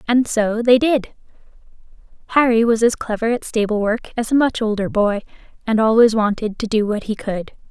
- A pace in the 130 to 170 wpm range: No, average, 185 wpm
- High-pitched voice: Yes, high, 225 Hz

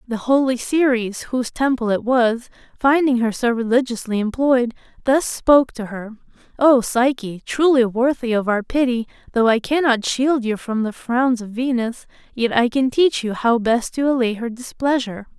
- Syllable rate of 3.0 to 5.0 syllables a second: Yes, 4.7 syllables/s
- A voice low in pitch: No, high, 245 Hz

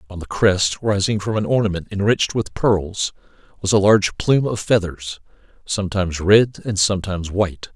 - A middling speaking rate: Yes, average, 160 wpm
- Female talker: No, male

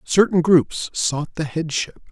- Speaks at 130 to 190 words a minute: Yes, average, 140 wpm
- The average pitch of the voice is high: No, medium, 165 Hz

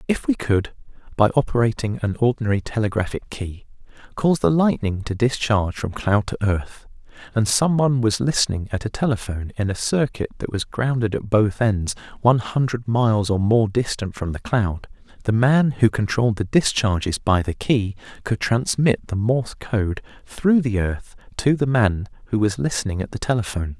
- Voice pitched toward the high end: No, low, 110 Hz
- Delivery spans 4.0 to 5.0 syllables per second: No, 5.2 syllables/s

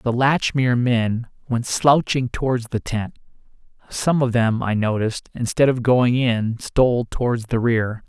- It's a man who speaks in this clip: Yes, male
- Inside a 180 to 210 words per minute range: No, average, 155 wpm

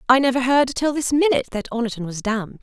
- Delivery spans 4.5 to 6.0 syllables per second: No, 6.4 syllables/s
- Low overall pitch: No, very high, 250 Hz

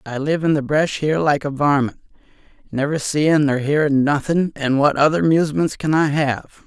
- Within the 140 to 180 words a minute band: No, average, 190 wpm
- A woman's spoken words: No, male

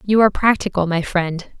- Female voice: Yes, female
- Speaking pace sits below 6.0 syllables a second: Yes, 5.7 syllables/s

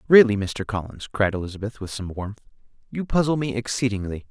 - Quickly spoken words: No, average, 165 wpm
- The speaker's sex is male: Yes, male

